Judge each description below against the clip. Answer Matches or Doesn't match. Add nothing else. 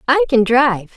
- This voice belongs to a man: Doesn't match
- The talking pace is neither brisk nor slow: Matches